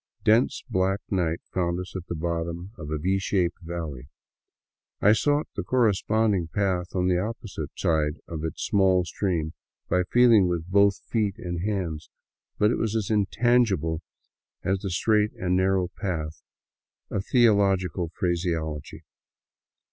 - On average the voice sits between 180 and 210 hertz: No, very low, 95 Hz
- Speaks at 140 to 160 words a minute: Yes, average, 150 wpm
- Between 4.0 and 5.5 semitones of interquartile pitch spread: No, average, 3.3 semitones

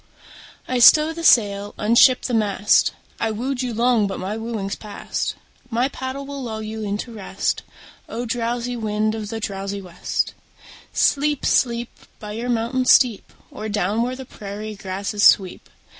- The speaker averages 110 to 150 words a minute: No, average, 160 wpm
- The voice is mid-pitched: No, high, 225 Hz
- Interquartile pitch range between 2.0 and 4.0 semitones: Yes, average, 3.0 semitones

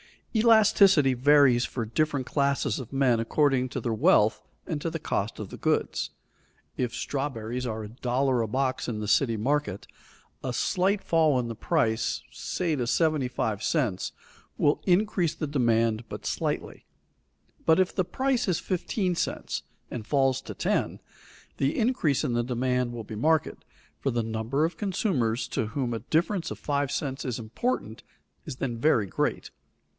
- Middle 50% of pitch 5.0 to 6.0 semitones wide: Yes, wide, 5.4 semitones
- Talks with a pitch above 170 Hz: No, low, 135 Hz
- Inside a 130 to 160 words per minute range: No, average, 170 wpm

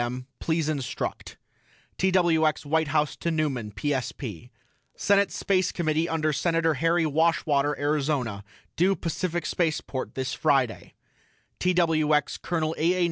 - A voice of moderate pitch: Yes, medium, 155 Hz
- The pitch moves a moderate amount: Yes, average, 3.0 semitones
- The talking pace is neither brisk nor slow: No, slow, 120 wpm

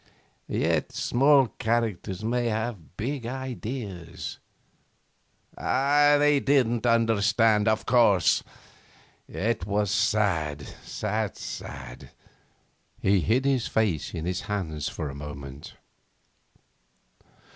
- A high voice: No, low, 110 Hz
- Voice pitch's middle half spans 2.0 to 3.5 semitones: No, average, 4.6 semitones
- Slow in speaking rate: Yes, slow, 90 wpm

